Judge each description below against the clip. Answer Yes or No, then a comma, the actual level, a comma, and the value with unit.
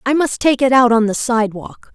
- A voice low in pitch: No, high, 245 Hz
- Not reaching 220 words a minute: No, fast, 245 wpm